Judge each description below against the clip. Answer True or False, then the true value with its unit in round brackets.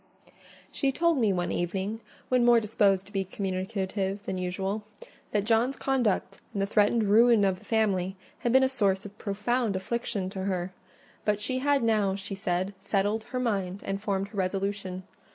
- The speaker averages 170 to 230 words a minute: True (175 wpm)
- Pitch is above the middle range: True (200 Hz)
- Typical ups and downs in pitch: True (3.0 semitones)